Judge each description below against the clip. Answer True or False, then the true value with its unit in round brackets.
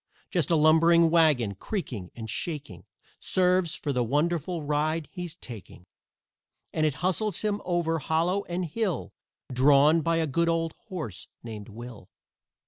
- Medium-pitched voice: True (160 Hz)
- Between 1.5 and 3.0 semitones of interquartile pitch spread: False (4.6 semitones)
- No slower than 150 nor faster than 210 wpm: False (140 wpm)